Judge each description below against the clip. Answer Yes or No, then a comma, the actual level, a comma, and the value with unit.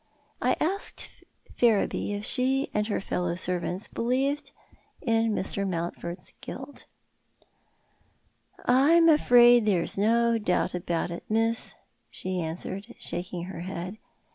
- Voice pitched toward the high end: Yes, high, 210 Hz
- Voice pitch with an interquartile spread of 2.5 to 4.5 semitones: No, average, 5.1 semitones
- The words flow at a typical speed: No, slow, 115 wpm